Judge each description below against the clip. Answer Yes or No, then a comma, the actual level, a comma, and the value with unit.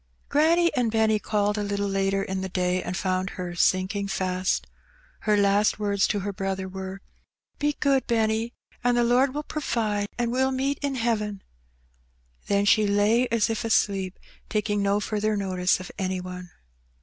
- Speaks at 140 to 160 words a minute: No, average, 170 wpm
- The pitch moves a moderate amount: Yes, average, 3.3 semitones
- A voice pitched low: No, high, 205 Hz